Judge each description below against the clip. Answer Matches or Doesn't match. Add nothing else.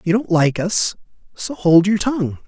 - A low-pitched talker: Doesn't match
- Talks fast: Doesn't match